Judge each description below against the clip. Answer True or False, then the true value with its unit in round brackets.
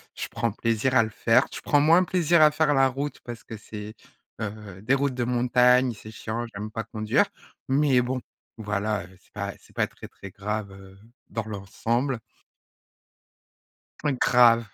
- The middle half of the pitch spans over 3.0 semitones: True (3.7 semitones)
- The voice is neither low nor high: False (115 Hz)